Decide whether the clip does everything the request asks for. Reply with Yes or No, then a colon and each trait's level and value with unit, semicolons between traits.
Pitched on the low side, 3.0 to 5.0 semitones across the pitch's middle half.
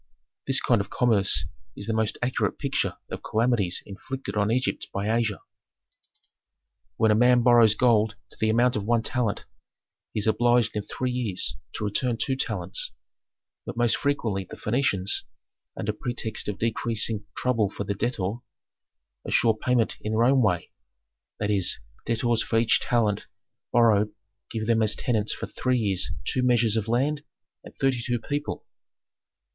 No: low, 115 Hz; narrow, 2.6 semitones